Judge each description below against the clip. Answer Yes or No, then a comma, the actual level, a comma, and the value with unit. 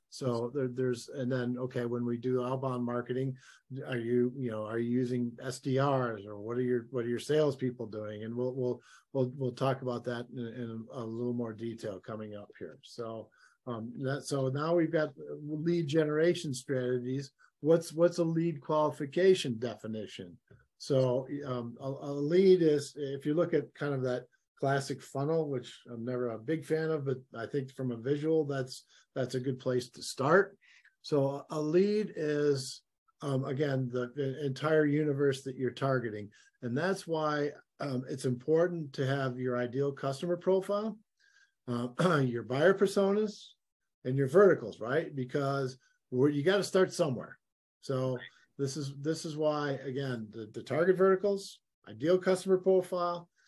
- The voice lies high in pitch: No, low, 135 Hz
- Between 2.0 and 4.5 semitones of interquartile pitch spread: Yes, average, 3.9 semitones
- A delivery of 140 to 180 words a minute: Yes, average, 170 wpm